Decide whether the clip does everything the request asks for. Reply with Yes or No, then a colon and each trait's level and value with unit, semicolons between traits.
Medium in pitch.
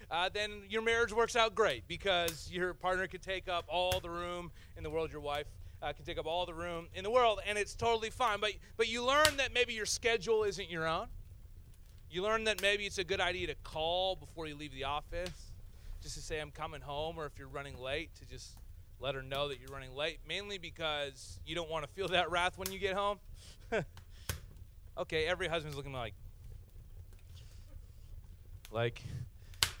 Yes: medium, 160 Hz